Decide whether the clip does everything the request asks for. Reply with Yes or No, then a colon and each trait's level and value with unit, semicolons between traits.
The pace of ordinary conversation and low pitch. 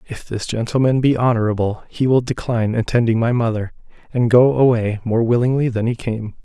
Yes: average, 175 wpm; low, 115 Hz